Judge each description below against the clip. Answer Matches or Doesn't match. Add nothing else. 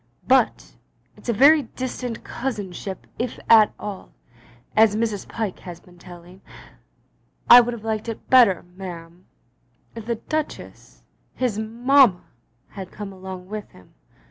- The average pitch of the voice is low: Doesn't match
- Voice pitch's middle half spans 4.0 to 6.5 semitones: Matches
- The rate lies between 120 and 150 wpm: Matches